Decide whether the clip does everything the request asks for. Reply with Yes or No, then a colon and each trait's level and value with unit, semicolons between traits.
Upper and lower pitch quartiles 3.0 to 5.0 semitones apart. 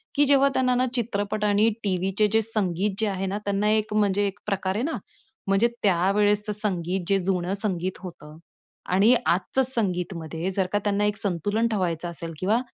No: narrow, 2.5 semitones